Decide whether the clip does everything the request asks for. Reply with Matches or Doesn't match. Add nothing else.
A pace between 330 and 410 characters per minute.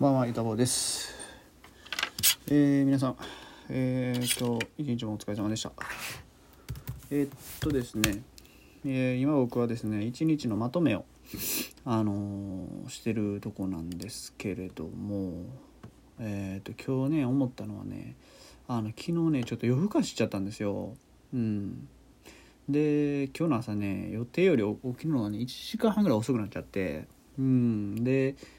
Doesn't match